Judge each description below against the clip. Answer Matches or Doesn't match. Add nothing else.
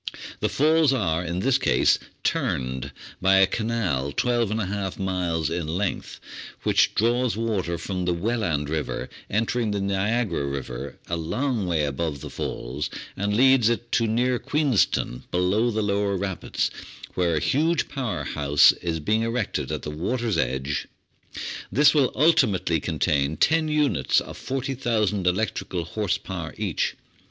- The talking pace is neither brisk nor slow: Matches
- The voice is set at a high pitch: Doesn't match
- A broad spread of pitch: Matches